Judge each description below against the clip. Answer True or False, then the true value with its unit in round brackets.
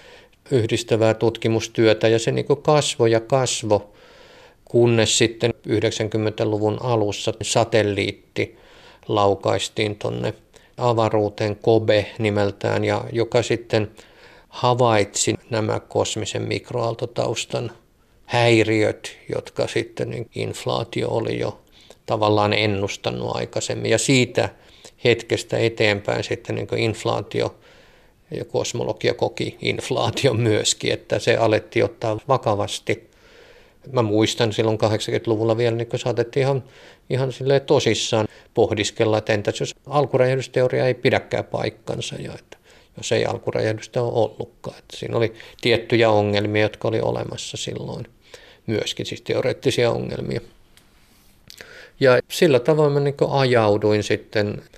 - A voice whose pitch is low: True (115 Hz)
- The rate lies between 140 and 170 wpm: False (110 wpm)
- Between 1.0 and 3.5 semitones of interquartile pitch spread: True (2.5 semitones)